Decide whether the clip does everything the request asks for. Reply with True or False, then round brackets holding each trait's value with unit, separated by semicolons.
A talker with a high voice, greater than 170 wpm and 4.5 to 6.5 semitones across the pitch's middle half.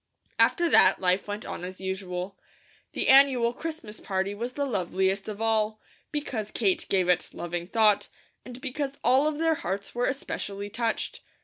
False (215 Hz; 165 wpm; 5.4 semitones)